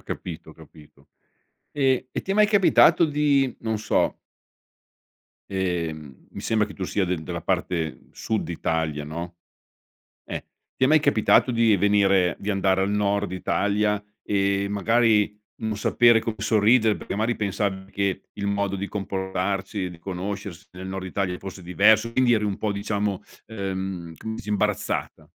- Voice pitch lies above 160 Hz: No, low, 100 Hz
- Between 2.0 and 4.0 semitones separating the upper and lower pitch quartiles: Yes, narrow, 2.6 semitones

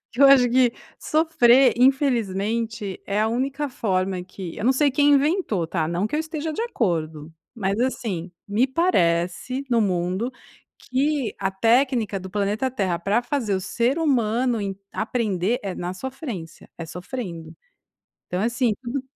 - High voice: Yes, high, 230 Hz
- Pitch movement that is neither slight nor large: No, wide, 5.7 semitones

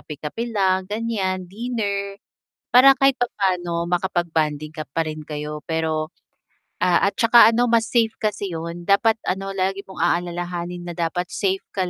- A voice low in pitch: No, medium, 185 Hz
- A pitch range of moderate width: Yes, average, 3.8 semitones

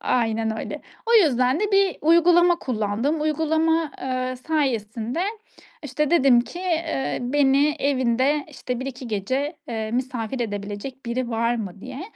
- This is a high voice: Yes, very high, 260 Hz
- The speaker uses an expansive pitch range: No, average, 4.7 semitones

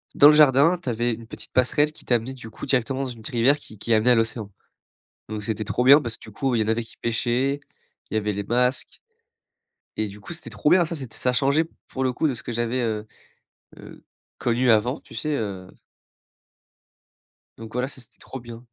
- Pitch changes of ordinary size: Yes, average, 3.2 semitones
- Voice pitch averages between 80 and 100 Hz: No, low, 120 Hz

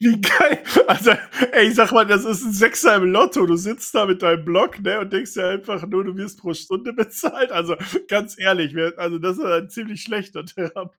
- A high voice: Yes, high, 195 Hz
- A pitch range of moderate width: Yes, average, 3.2 semitones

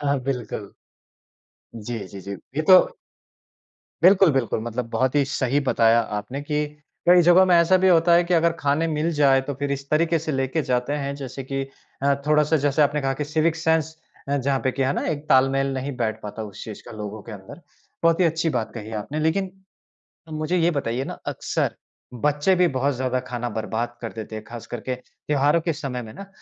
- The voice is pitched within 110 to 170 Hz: Yes, medium, 140 Hz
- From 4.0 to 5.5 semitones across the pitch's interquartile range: Yes, average, 4.4 semitones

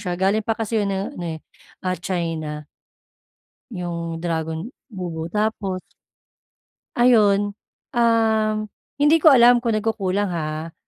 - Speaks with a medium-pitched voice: No, high, 195 Hz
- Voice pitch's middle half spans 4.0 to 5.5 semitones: Yes, average, 4.5 semitones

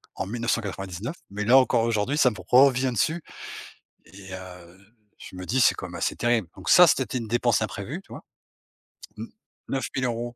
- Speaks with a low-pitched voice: Yes, low, 115 Hz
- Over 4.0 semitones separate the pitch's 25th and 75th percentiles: Yes, average, 4.7 semitones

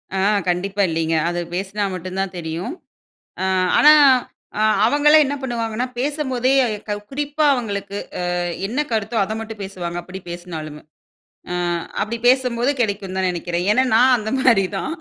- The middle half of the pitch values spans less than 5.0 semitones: No, wide, 5.4 semitones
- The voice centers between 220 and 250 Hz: No, high, 205 Hz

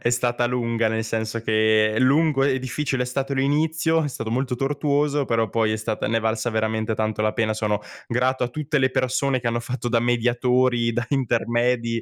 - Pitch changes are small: No, average, 3.0 semitones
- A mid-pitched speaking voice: No, low, 120 Hz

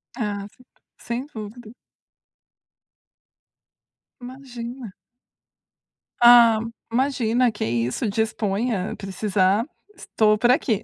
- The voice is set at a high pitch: Yes, high, 225 Hz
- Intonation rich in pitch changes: No, average, 3.0 semitones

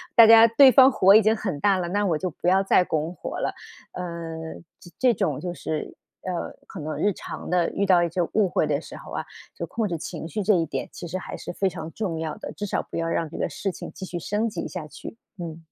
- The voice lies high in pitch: No, medium, 180 Hz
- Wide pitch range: No, average, 3.8 semitones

